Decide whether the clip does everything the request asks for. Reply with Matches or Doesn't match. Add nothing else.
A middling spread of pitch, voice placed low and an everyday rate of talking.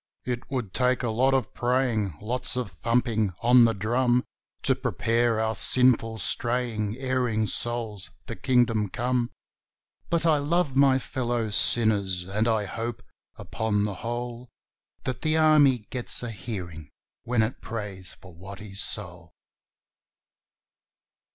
Doesn't match